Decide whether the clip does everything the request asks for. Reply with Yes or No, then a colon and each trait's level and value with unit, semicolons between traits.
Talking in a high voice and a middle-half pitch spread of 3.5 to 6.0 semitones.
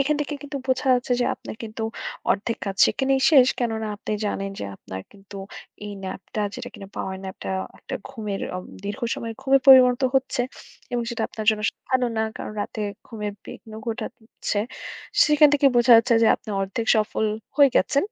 Yes: high, 230 Hz; average, 3.9 semitones